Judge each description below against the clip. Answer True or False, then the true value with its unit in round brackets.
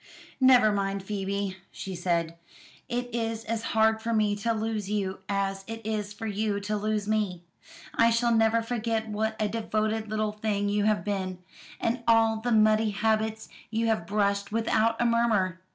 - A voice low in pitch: False (215 Hz)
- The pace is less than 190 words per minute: True (170 wpm)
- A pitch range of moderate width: False (1.9 semitones)